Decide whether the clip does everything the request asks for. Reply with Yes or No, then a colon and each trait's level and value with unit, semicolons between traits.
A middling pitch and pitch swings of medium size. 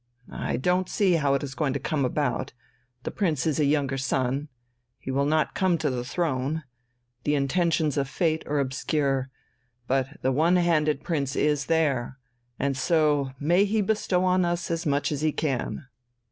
Yes: medium, 150 Hz; average, 3.4 semitones